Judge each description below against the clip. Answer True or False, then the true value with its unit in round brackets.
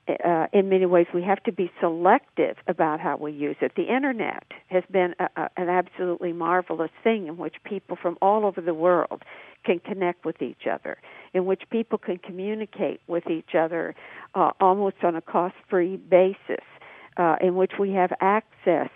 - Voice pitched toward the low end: False (180 Hz)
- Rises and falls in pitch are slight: True (2.1 semitones)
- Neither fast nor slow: True (185 wpm)